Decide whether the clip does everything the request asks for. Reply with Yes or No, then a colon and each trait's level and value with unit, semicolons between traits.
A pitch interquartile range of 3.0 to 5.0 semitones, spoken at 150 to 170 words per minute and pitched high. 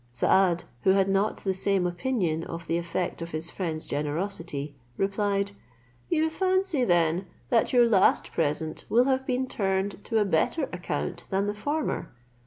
No: wide, 5.4 semitones; average, 160 wpm; high, 195 Hz